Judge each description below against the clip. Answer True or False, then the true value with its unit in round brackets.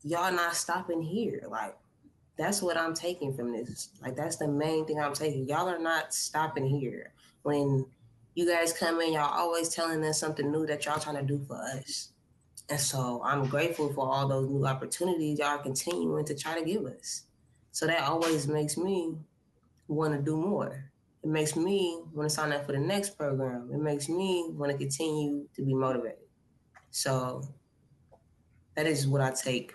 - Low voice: False (150 Hz)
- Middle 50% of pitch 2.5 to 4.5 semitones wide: True (3.0 semitones)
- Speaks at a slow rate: False (185 wpm)